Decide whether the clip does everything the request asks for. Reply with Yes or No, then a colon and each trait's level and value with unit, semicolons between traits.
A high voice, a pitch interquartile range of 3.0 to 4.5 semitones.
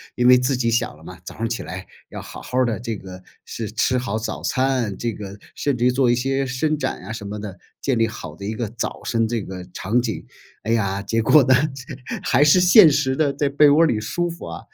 No: low, 120 Hz; average, 3.8 semitones